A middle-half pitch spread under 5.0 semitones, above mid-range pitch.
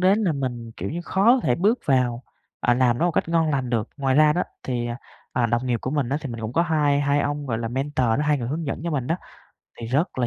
No: average, 4.1 semitones; low, 135 Hz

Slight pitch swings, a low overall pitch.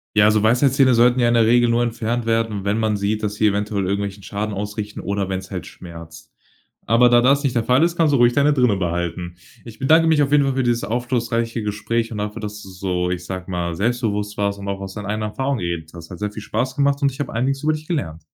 No: average, 3.7 semitones; low, 110 Hz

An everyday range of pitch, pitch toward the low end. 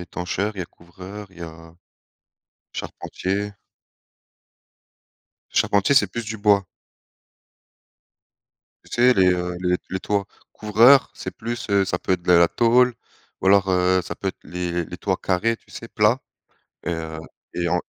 Yes: average, 3.3 semitones; very low, 95 Hz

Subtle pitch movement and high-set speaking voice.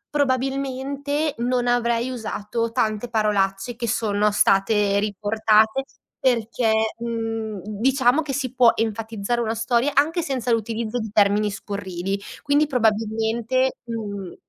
No: average, 3.1 semitones; high, 230 Hz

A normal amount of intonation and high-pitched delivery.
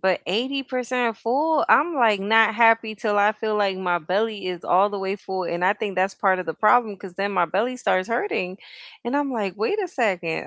Yes: average, 4.0 semitones; high, 210 Hz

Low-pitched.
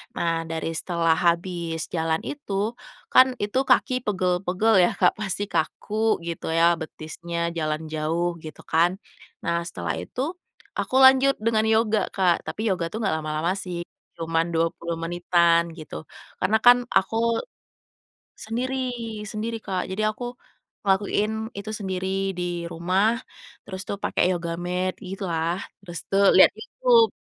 No: medium, 180 Hz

